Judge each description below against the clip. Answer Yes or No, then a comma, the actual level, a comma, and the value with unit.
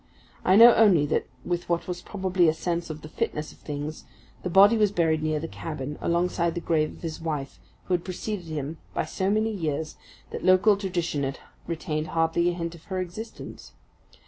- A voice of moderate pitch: Yes, medium, 170 Hz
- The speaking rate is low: No, average, 200 wpm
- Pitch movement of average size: Yes, average, 3.0 semitones